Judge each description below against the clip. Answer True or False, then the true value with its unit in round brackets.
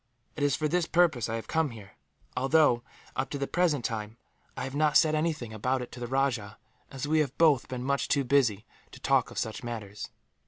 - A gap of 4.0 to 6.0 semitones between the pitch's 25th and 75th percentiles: True (4.4 semitones)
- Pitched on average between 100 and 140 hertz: True (135 Hz)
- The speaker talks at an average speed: False (220 wpm)